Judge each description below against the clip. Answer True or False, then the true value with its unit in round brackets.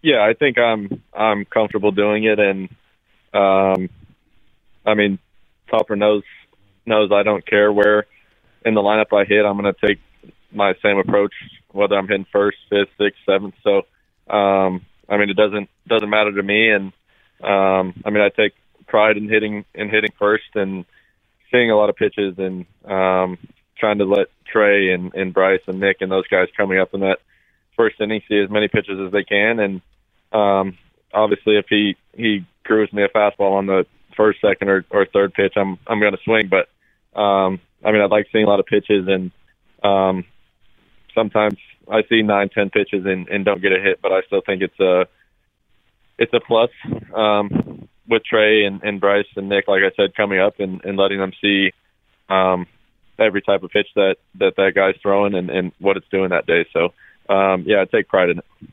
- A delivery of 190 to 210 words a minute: True (195 wpm)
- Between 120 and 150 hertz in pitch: False (100 Hz)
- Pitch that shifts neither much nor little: False (1.6 semitones)